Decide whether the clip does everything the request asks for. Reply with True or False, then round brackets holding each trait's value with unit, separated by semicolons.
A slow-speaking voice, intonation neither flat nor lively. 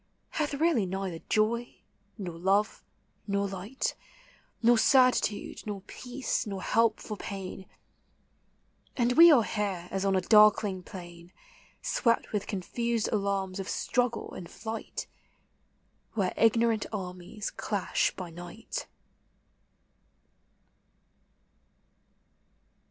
True (105 wpm; 3.5 semitones)